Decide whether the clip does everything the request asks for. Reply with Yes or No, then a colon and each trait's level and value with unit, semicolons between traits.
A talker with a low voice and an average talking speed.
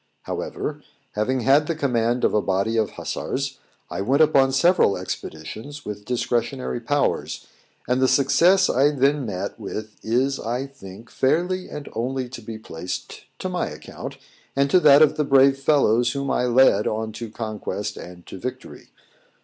Yes: low, 125 Hz; average, 165 wpm